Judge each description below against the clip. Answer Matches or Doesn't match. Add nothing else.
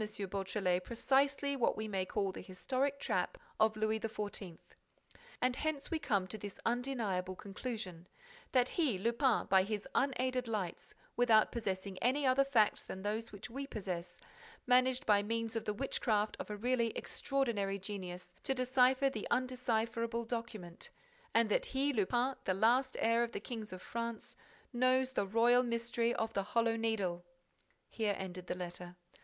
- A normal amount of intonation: Matches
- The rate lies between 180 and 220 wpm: Doesn't match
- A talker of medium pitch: Doesn't match